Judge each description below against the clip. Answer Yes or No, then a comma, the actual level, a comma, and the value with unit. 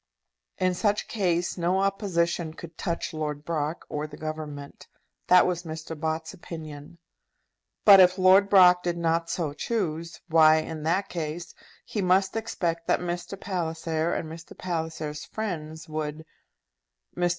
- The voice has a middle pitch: Yes, medium, 170 Hz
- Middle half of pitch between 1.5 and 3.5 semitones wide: Yes, narrow, 2.5 semitones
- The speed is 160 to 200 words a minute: No, average, 140 wpm